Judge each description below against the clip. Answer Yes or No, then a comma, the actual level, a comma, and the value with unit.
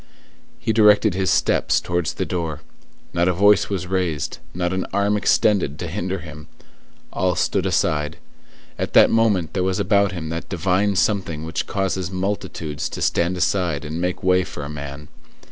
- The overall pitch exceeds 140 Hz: No, very low, 90 Hz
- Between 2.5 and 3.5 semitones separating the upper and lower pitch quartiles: Yes, average, 3.1 semitones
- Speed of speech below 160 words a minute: No, average, 170 wpm